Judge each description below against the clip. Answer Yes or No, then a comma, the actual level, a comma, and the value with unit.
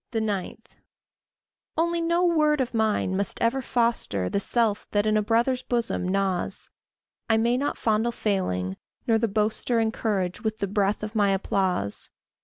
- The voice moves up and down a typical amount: Yes, average, 3.2 semitones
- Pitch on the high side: Yes, high, 220 Hz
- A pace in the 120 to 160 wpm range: Yes, average, 155 wpm